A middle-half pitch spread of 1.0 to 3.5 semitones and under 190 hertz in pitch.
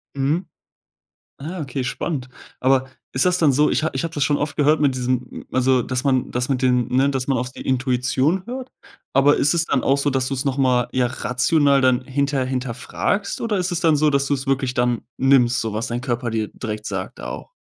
Yes: narrow, 2.5 semitones; low, 135 Hz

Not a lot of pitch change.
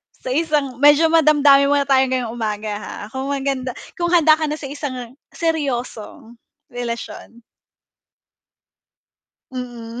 No: average, 3.5 semitones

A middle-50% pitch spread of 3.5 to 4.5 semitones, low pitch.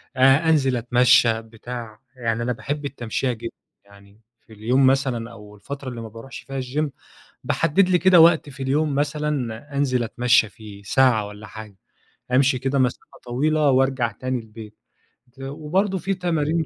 Yes: average, 4.1 semitones; low, 130 Hz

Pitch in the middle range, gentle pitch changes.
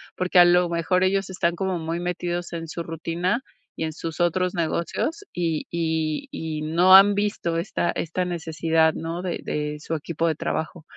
Yes: medium, 170 Hz; narrow, 2.0 semitones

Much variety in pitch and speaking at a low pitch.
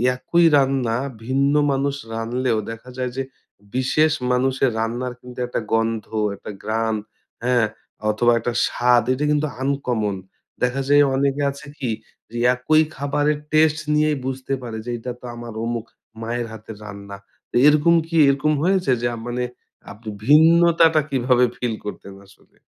No: average, 3.6 semitones; low, 125 Hz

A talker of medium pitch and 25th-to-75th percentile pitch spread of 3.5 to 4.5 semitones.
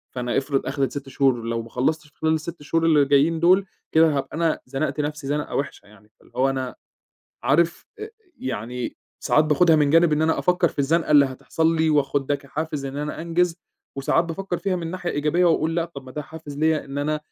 No: medium, 150 Hz; average, 3.0 semitones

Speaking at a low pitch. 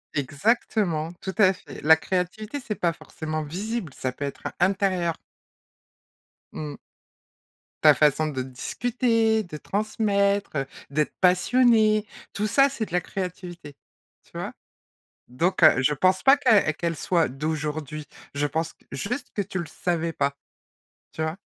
No: medium, 175 Hz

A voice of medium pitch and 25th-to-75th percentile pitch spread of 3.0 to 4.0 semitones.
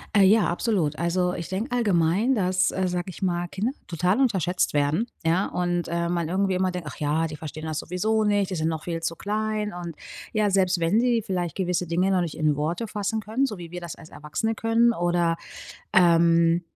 Yes: medium, 180 Hz; average, 3.4 semitones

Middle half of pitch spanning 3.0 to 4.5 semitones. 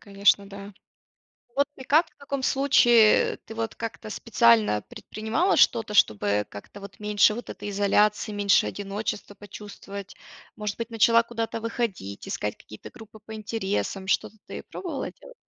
No: narrow, 2.5 semitones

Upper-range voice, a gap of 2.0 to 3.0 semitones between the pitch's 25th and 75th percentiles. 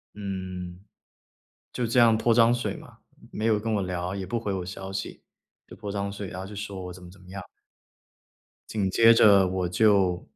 No: low, 100 Hz; average, 2.7 semitones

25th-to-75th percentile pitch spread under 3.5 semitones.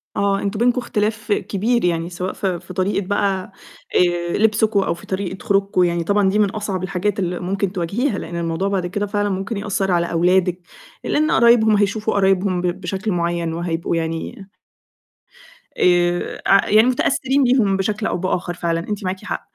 Yes: average, 2.8 semitones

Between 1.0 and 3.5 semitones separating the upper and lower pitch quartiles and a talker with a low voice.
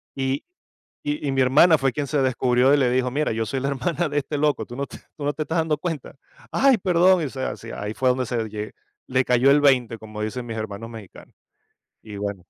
No: average, 4.2 semitones; low, 130 Hz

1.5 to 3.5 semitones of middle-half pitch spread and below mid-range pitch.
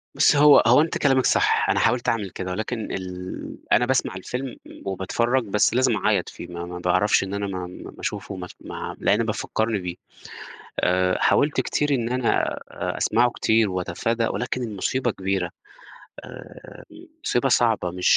No: average, 5.0 semitones; low, 105 Hz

